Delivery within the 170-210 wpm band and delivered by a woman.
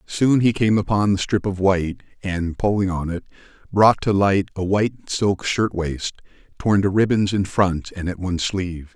No: average, 190 wpm; male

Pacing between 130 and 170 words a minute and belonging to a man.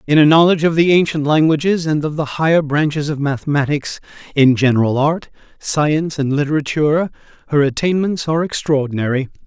Yes: average, 150 wpm; male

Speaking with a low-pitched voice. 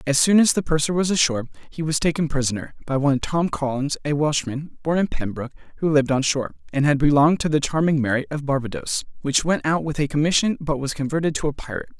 No: medium, 150 Hz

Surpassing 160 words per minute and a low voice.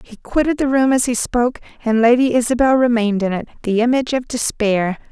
No: average, 200 wpm; high, 240 Hz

